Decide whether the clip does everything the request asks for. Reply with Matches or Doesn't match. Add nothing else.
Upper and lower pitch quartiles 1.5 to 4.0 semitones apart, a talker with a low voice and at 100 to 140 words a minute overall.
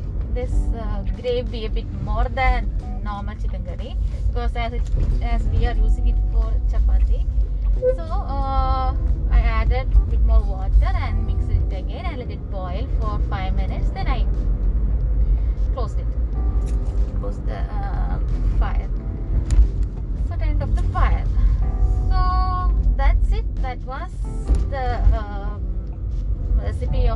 Doesn't match